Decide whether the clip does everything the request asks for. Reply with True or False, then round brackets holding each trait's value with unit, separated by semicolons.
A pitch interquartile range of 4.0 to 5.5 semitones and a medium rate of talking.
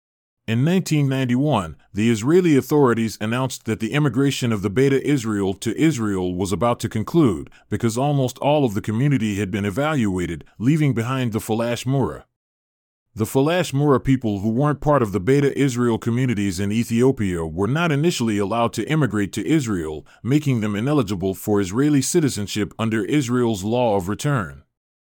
True (4.8 semitones; 160 wpm)